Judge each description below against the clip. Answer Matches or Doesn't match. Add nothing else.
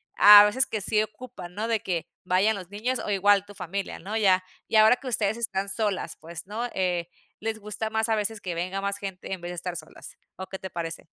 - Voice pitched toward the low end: Doesn't match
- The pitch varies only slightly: Doesn't match